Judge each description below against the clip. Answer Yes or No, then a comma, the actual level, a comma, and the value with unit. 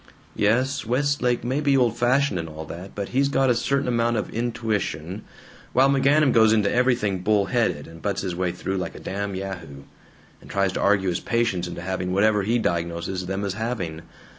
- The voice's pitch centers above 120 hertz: No, low, 105 Hz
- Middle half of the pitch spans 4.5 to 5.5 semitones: Yes, average, 4.8 semitones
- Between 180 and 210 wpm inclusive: Yes, average, 195 wpm